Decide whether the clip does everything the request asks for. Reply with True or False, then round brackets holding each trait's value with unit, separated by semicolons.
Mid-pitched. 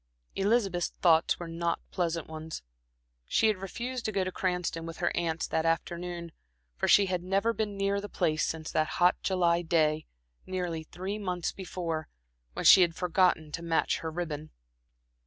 True (175 Hz)